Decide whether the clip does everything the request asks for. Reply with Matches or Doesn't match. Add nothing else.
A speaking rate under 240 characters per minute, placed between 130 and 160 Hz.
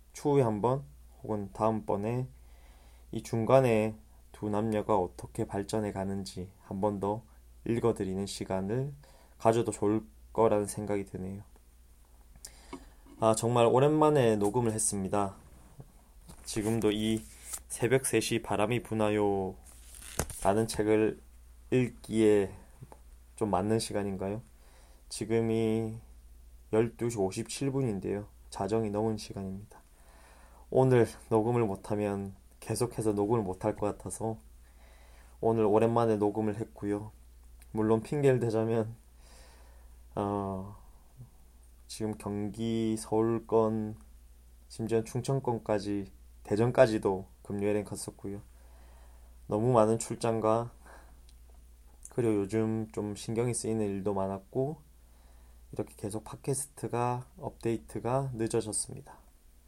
Doesn't match